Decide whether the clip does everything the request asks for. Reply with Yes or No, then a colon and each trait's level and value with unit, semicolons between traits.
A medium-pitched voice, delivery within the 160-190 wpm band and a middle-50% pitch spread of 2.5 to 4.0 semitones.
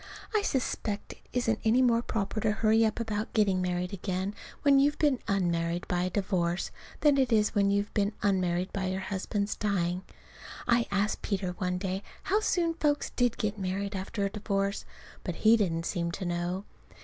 No: high, 200 Hz; average, 185 wpm; average, 3.4 semitones